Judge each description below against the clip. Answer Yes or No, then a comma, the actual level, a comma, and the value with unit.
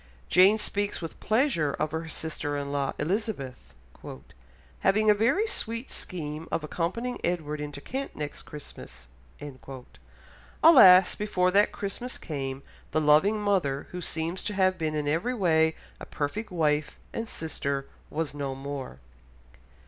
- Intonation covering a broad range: Yes, wide, 5.8 semitones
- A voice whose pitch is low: No, medium, 165 Hz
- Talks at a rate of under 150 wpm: Yes, average, 140 wpm